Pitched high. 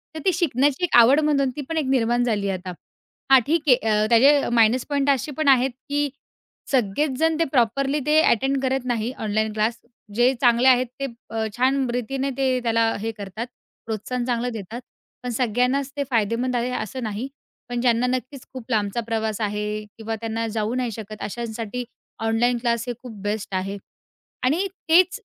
Yes: high, 245 Hz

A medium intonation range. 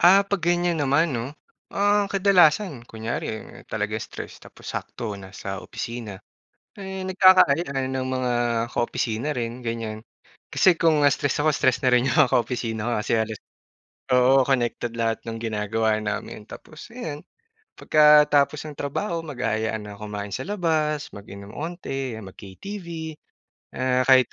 No: wide, 6.2 semitones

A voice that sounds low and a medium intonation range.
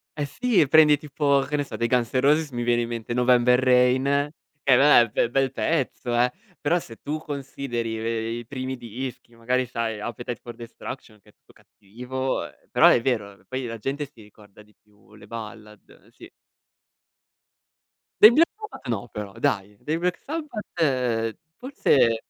Yes: low, 125 Hz; average, 3.7 semitones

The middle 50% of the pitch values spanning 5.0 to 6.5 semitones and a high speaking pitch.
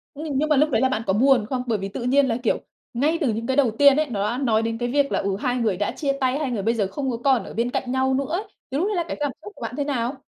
No: average, 3.7 semitones; very high, 260 Hz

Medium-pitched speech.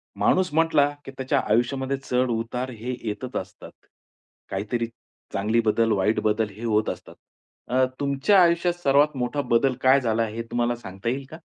No: low, 125 Hz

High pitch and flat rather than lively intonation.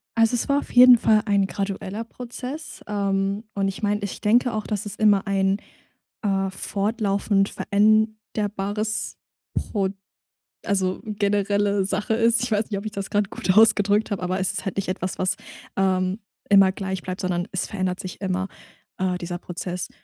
Yes: high, 200 Hz; narrow, 2.1 semitones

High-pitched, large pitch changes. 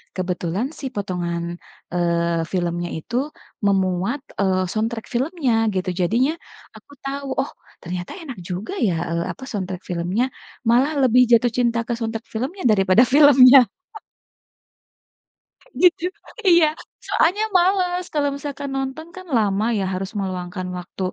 Yes: high, 225 Hz; wide, 7.1 semitones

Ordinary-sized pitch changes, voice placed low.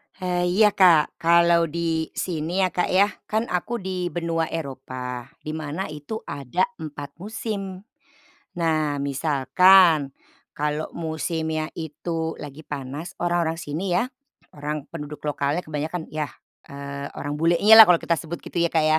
No: average, 3.1 semitones; medium, 160 Hz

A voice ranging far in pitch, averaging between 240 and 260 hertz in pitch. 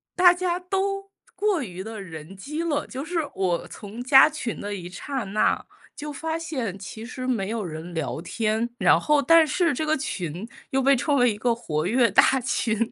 Yes: wide, 7.7 semitones; high, 245 Hz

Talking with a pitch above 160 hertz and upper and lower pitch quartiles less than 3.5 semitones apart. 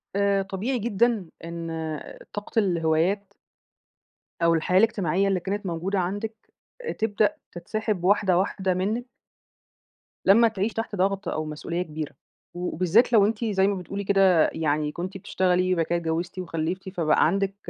Yes: high, 190 Hz; average, 3.0 semitones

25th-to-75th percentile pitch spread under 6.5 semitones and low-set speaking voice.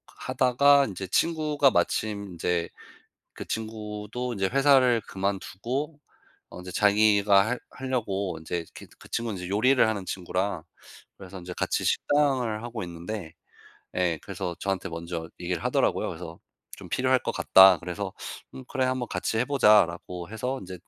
Yes: average, 5.3 semitones; low, 100 Hz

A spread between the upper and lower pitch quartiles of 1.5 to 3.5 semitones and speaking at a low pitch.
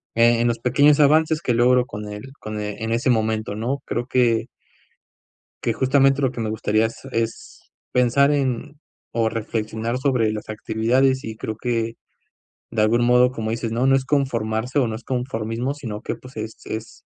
Yes: average, 2.8 semitones; low, 115 Hz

